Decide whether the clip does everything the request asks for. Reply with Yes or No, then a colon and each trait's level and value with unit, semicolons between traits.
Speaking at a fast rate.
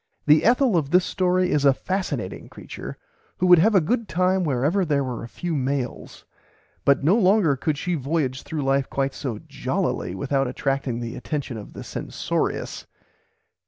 No: average, 170 wpm